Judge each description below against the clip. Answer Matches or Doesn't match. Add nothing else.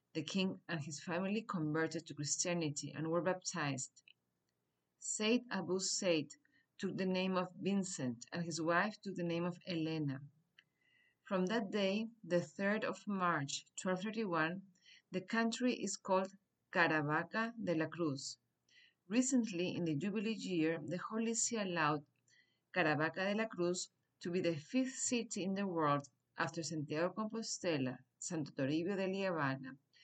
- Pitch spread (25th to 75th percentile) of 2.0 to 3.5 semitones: Doesn't match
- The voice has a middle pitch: Matches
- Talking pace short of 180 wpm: Matches